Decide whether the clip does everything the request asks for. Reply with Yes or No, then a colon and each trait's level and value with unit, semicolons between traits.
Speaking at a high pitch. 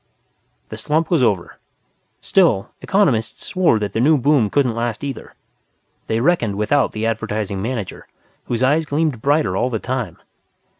No: low, 120 Hz